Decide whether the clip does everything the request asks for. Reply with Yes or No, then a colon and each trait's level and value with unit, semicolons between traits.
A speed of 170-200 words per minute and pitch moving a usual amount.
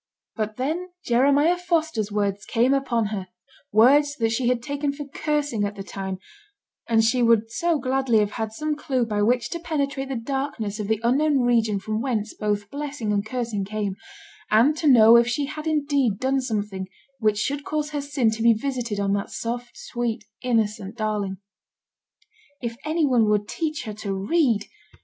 Yes: average, 180 wpm; average, 4.9 semitones